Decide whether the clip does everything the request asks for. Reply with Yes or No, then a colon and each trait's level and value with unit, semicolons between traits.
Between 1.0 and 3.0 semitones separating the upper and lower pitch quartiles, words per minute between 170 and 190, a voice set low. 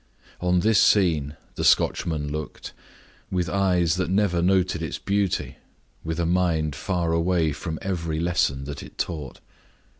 No: narrow, 2.6 semitones; average, 145 wpm; very low, 85 Hz